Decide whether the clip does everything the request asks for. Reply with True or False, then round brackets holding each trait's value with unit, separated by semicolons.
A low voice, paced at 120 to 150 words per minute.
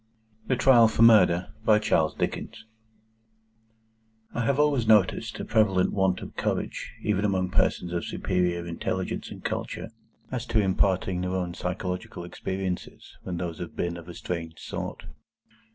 True (95 Hz; 135 wpm)